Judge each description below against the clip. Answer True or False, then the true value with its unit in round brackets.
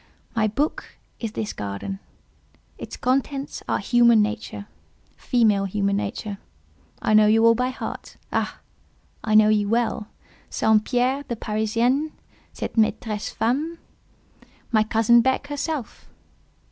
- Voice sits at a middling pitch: False (225 Hz)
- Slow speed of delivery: True (115 wpm)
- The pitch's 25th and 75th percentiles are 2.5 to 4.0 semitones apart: True (2.8 semitones)